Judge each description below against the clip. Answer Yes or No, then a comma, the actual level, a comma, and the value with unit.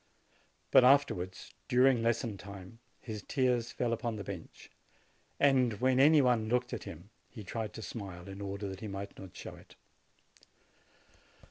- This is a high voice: No, low, 110 Hz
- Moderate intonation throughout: Yes, average, 4.1 semitones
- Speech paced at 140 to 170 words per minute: Yes, average, 155 wpm